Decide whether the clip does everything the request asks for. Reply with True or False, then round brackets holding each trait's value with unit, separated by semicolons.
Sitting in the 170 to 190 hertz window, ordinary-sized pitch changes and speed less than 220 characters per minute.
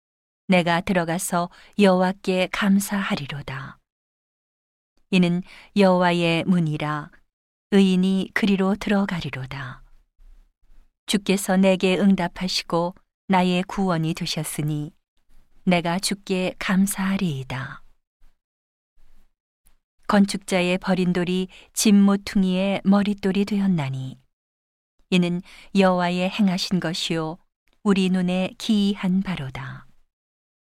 True (185 Hz; 3.7 semitones; 210 characters per minute)